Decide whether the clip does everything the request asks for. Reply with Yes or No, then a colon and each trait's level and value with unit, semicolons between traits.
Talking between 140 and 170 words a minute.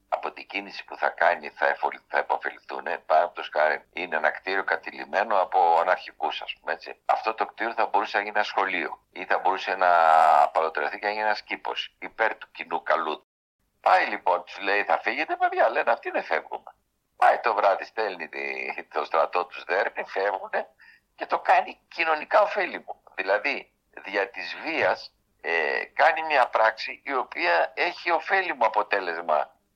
Yes: average, 165 wpm